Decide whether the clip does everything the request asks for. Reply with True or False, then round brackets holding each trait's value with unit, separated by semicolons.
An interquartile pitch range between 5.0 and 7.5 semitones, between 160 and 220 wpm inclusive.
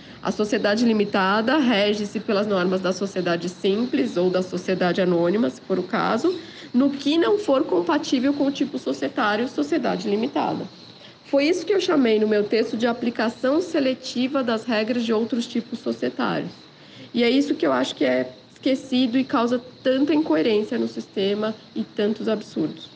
True (5.3 semitones; 165 wpm)